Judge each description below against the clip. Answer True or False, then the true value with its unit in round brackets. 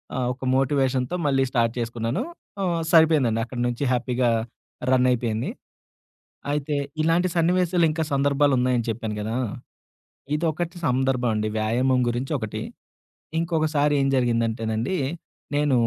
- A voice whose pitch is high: False (130 Hz)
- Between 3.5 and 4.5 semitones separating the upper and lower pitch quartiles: True (4.0 semitones)